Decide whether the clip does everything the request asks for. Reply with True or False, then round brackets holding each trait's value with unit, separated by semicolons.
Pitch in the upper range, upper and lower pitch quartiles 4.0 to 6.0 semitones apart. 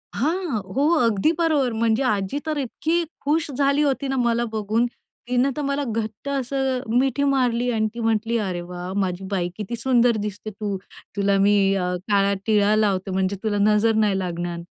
True (225 Hz; 5.1 semitones)